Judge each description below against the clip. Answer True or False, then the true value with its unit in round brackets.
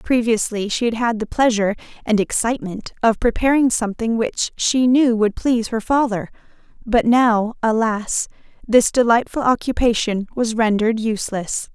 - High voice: True (225 Hz)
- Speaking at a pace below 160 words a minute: True (140 wpm)